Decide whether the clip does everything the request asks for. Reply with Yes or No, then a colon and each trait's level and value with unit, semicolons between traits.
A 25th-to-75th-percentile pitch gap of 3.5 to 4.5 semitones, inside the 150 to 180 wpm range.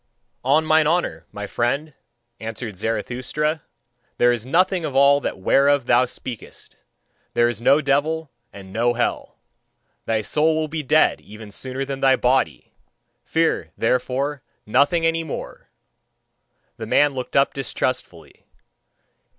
No: average, 4.2 semitones; slow, 135 wpm